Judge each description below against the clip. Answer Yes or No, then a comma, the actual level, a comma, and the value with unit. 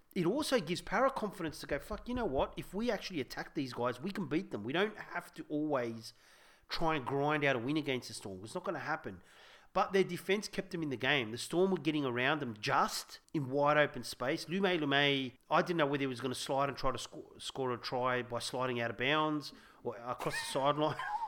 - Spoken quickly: Yes, fast, 245 wpm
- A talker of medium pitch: Yes, medium, 150 Hz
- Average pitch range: No, wide, 5.9 semitones